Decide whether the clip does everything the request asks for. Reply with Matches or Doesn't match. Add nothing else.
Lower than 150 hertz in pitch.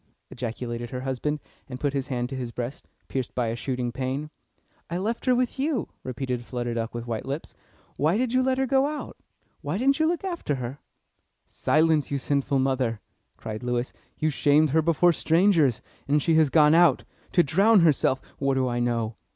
Matches